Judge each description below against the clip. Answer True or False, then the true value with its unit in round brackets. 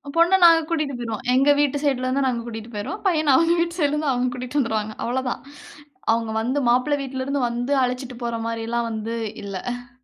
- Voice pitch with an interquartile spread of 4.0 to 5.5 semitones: False (3.6 semitones)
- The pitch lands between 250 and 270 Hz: True (255 Hz)